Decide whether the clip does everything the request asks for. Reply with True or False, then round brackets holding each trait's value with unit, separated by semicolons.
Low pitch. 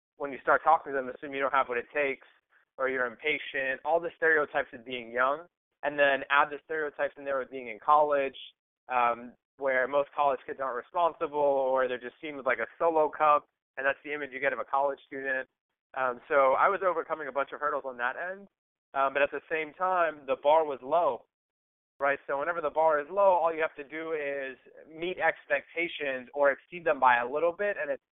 False (145 Hz)